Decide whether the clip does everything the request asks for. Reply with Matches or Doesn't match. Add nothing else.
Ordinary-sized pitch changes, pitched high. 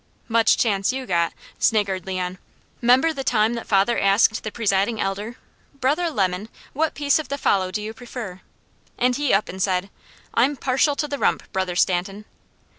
Matches